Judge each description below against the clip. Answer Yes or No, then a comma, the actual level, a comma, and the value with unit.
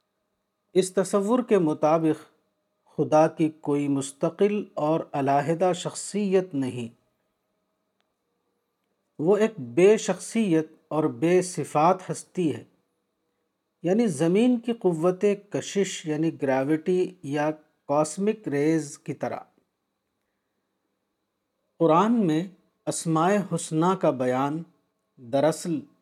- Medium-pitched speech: Yes, medium, 160 Hz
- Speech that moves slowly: Yes, slow, 90 wpm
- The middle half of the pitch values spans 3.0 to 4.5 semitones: Yes, average, 4.1 semitones